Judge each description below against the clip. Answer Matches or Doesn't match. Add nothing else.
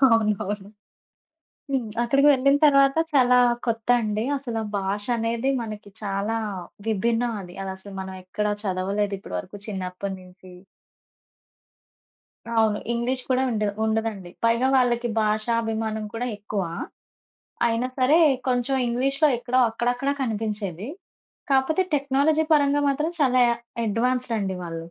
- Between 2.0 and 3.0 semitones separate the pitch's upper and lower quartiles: Doesn't match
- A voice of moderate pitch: Doesn't match